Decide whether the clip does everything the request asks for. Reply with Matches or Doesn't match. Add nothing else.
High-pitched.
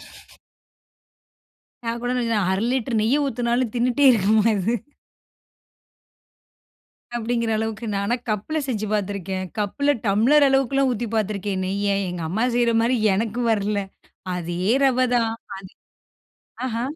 Matches